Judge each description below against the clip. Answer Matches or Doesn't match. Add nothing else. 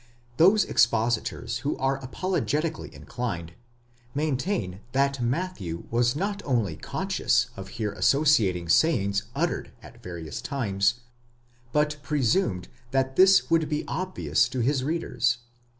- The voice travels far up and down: Matches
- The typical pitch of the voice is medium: Doesn't match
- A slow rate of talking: Matches